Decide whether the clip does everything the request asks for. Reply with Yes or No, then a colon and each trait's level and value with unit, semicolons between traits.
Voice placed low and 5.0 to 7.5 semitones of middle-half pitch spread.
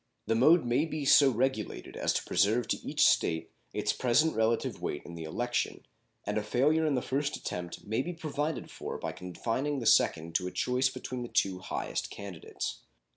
Yes: low, 120 Hz; wide, 5.6 semitones